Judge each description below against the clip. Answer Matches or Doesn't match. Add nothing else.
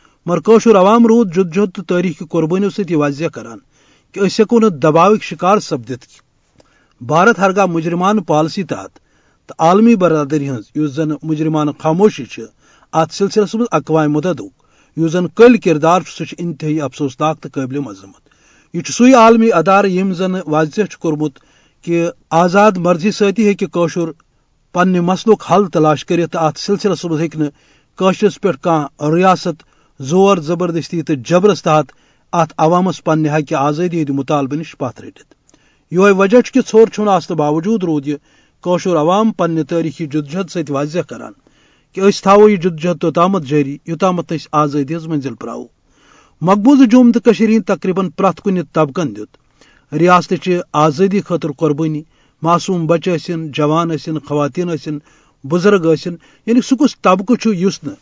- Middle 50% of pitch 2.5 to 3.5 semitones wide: Doesn't match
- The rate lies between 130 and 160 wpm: Matches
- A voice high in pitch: Doesn't match